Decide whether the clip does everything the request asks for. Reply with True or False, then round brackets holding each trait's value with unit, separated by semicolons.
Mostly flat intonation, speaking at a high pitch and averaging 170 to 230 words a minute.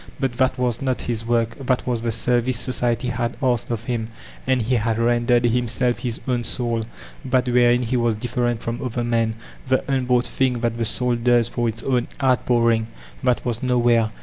False (1.3 semitones; 120 Hz; 200 wpm)